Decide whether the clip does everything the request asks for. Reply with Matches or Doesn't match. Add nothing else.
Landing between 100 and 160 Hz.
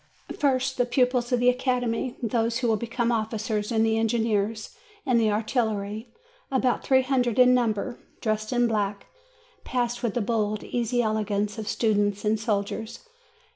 Doesn't match